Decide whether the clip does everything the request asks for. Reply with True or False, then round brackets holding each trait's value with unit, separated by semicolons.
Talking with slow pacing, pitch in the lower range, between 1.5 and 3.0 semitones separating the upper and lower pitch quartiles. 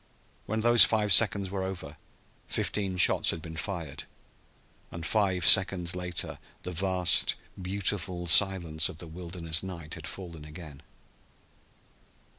True (125 wpm; 90 Hz; 2.7 semitones)